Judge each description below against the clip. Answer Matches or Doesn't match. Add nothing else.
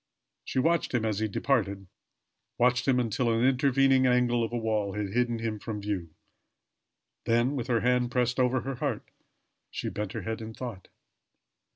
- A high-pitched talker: Doesn't match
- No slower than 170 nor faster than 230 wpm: Matches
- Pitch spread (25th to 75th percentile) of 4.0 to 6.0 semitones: Doesn't match